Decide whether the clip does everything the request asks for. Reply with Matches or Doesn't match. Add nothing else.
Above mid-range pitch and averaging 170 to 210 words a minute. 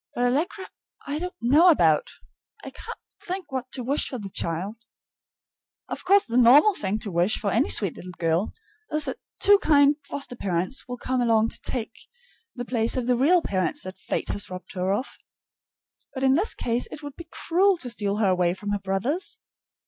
Matches